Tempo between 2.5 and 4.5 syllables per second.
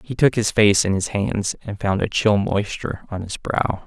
No: 4.7 syllables/s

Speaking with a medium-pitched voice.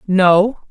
No: high, 195 Hz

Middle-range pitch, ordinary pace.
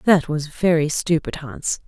Yes: medium, 160 Hz; average, 160 wpm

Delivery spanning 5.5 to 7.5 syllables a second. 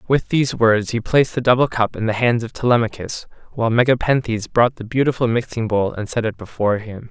Yes: 6.0 syllables/s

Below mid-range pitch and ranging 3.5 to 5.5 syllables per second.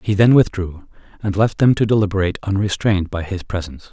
No: low, 100 Hz; 6.3 syllables/s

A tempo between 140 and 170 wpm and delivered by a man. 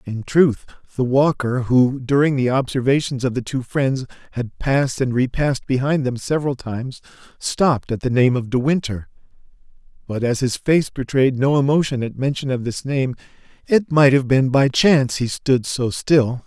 No: average, 180 wpm; male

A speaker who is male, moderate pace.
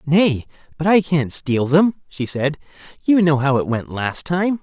Yes: male; average, 195 wpm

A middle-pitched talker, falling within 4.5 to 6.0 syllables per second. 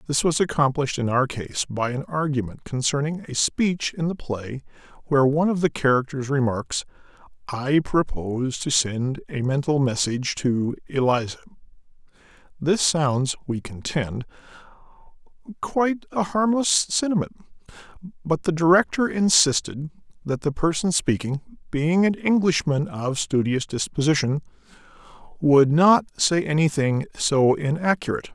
Yes: medium, 150 Hz; 4.7 syllables/s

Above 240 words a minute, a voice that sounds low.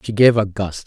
Yes: fast, 275 wpm; low, 100 Hz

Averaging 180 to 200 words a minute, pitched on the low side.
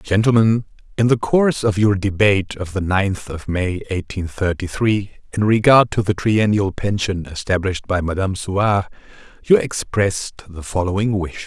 No: average, 150 wpm; low, 100 Hz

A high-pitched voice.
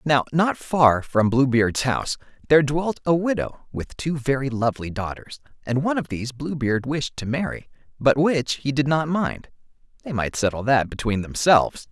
No: low, 135 Hz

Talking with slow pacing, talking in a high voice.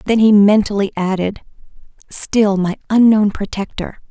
Yes: slow, 100 wpm; high, 205 Hz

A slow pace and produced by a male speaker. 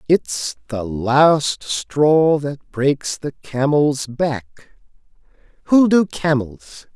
Yes: slow, 105 wpm; male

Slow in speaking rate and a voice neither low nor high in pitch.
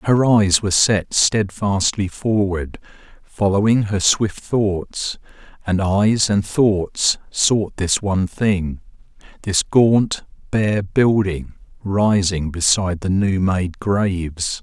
No: slow, 115 wpm; low, 100 Hz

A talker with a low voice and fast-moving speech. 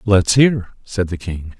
No: low, 100 Hz; average, 190 wpm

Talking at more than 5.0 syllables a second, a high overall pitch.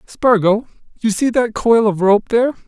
No: 4.8 syllables/s; high, 220 Hz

